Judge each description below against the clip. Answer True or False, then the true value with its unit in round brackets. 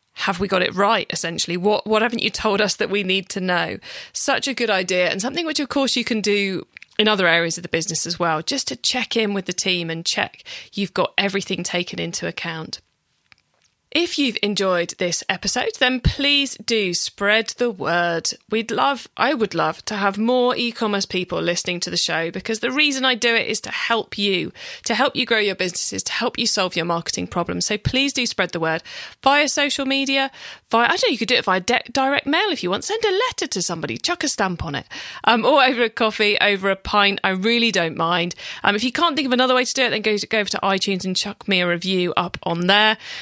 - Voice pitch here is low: False (205 Hz)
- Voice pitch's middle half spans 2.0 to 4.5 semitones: False (5.3 semitones)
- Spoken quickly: True (240 wpm)